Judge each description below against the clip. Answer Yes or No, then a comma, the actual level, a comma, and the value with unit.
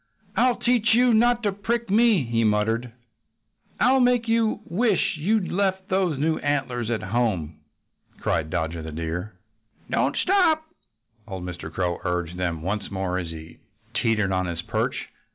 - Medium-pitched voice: No, low, 120 Hz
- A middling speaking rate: Yes, average, 155 wpm